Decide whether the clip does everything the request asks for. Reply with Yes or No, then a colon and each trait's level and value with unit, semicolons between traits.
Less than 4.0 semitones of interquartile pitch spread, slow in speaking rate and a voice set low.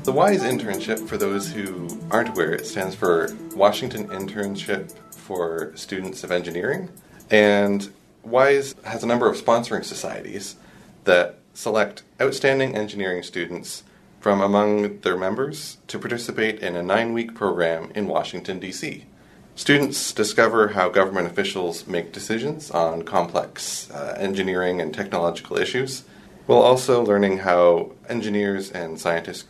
No: average, 4.3 semitones; slow, 130 wpm; low, 100 Hz